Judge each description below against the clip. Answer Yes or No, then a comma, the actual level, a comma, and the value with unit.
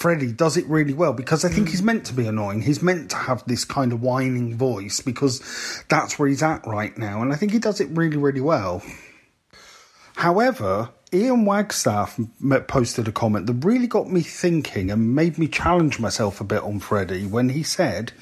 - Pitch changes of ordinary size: No, wide, 6.3 semitones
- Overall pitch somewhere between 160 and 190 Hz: No, low, 135 Hz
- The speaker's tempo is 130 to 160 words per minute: No, average, 200 wpm